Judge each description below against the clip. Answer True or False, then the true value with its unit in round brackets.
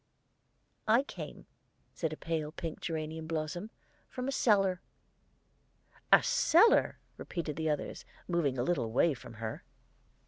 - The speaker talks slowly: True (130 wpm)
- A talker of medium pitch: True (160 Hz)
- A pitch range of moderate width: True (4.3 semitones)